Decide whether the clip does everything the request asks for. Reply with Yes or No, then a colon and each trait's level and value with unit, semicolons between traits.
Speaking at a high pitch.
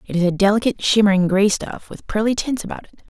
Yes: high, 205 Hz